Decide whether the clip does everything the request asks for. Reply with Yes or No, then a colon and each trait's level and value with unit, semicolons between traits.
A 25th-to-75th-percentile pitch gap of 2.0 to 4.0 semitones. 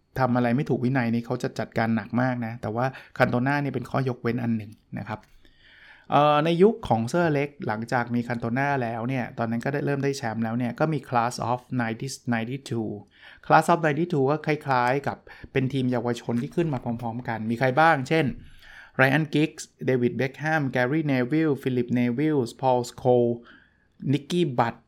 Yes: average, 3.1 semitones